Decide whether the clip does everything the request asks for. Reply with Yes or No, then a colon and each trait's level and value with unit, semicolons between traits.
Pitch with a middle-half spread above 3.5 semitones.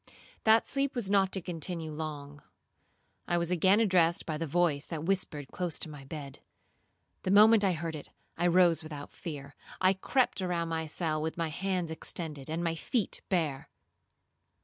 No: average, 3.2 semitones